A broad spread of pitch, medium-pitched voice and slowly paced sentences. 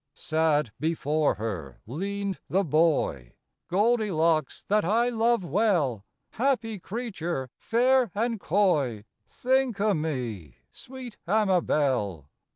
Yes: wide, 7.9 semitones; medium, 175 Hz; slow, 105 wpm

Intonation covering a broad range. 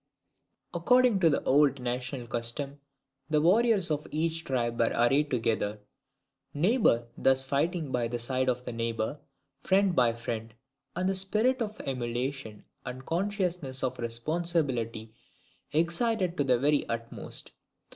Yes: wide, 6.3 semitones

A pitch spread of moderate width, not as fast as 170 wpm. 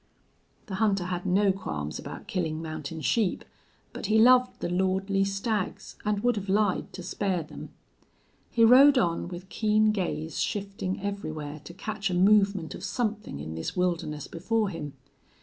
Yes: average, 3.8 semitones; average, 160 wpm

